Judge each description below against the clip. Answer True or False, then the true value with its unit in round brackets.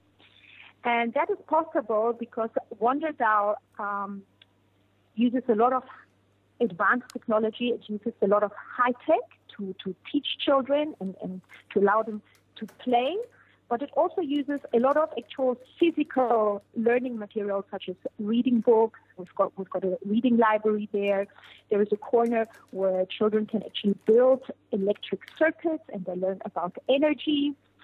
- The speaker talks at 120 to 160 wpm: True (150 wpm)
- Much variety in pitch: False (4.3 semitones)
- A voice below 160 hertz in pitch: False (225 Hz)